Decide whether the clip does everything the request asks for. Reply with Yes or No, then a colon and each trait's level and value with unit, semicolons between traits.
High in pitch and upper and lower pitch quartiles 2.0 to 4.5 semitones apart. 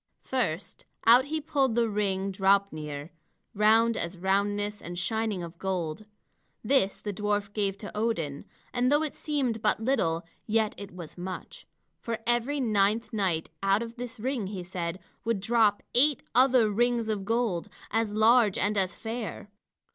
Yes: high, 210 Hz; average, 3.5 semitones